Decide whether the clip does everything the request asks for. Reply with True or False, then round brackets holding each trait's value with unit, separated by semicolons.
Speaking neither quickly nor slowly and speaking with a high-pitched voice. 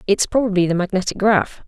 True (180 wpm; 195 Hz)